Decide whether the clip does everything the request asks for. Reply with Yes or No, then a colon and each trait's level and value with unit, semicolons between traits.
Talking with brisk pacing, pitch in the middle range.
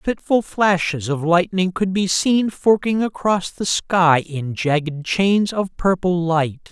No: average, 150 wpm; medium, 180 Hz